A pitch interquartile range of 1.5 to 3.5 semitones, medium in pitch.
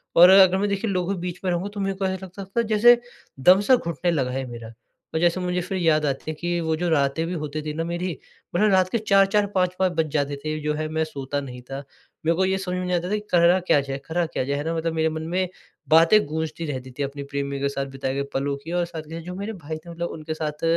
No: average, 3.9 semitones; medium, 165 Hz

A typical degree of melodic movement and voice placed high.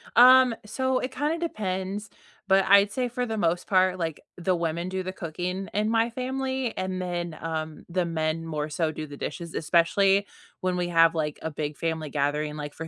No: average, 4.5 semitones; medium, 180 Hz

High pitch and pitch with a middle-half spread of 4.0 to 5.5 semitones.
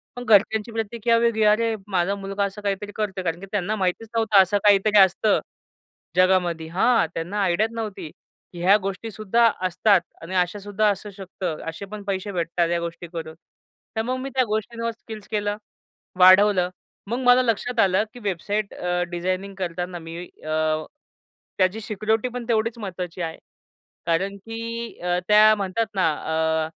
No: high, 200 Hz; average, 3.5 semitones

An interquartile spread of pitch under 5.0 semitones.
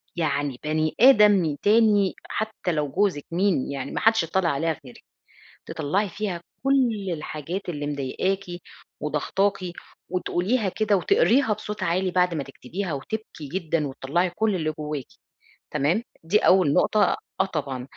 No: wide, 5.4 semitones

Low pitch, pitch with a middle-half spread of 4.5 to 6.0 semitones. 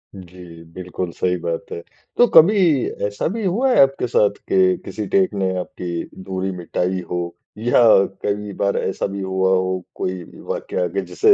Yes: very low, 95 Hz; average, 5.2 semitones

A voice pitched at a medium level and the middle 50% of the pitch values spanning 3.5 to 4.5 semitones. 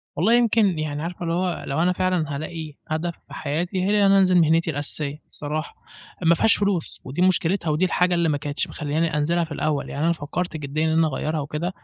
No: medium, 165 Hz; average, 3.0 semitones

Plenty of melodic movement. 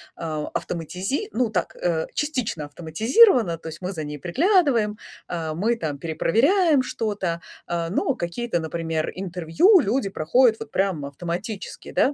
Yes: wide, 6.6 semitones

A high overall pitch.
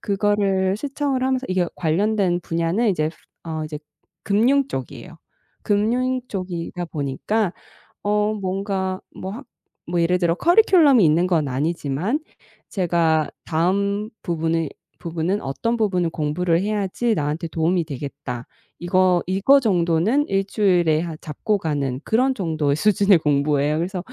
No: medium, 180 Hz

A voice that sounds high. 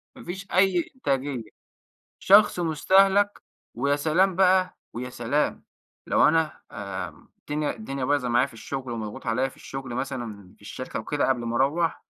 No: medium, 140 Hz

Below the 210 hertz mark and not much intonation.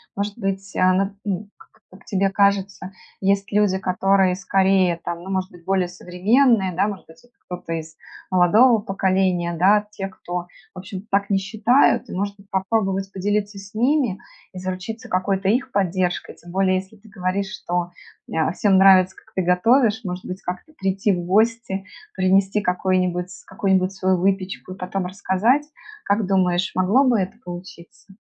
Yes: high, 190 Hz; narrow, 1.7 semitones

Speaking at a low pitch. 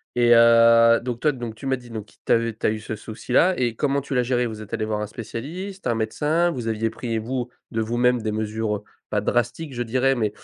Yes: low, 115 Hz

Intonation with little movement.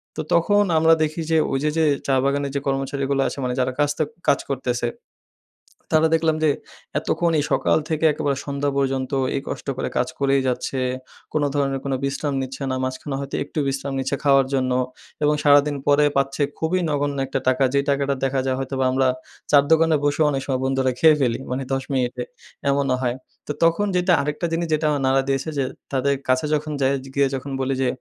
Yes: narrow, 1.9 semitones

